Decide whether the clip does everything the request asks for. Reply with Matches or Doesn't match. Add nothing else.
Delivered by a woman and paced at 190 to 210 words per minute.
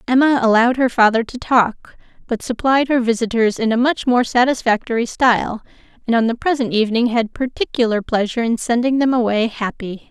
Doesn't match